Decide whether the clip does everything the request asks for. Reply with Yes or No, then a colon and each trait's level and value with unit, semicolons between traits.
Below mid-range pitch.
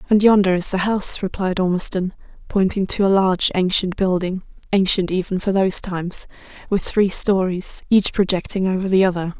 No: high, 190 Hz